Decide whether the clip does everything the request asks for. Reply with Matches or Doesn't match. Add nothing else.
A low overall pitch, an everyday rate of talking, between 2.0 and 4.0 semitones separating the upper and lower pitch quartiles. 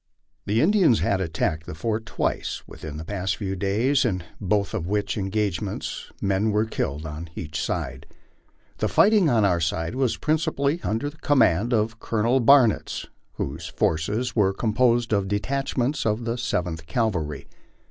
Doesn't match